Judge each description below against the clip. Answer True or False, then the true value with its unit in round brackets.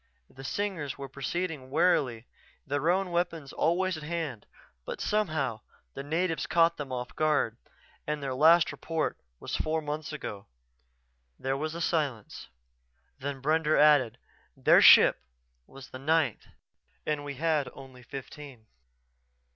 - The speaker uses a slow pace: True (130 wpm)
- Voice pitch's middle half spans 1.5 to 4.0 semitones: True (3.4 semitones)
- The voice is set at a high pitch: False (150 Hz)